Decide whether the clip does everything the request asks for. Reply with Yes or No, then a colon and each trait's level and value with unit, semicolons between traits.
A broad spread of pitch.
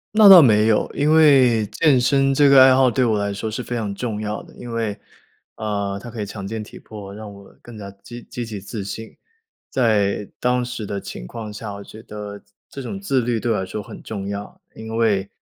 No: average, 3.3 semitones